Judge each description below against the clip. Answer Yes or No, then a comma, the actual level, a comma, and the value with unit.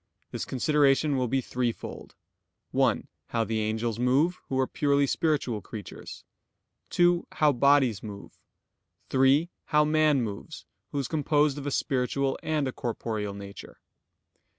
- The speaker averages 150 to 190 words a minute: No, slow, 135 wpm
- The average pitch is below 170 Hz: Yes, low, 135 Hz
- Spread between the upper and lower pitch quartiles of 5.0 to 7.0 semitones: No, average, 4.2 semitones